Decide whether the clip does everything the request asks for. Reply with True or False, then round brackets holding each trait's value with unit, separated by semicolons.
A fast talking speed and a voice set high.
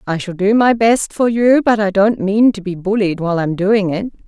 True (255 wpm; 205 Hz)